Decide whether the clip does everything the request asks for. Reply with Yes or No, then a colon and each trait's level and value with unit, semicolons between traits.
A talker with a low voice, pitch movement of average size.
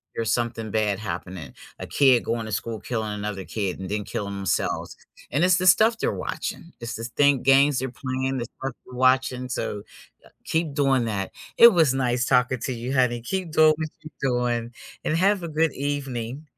Yes: low, 125 Hz; average, 4.0 semitones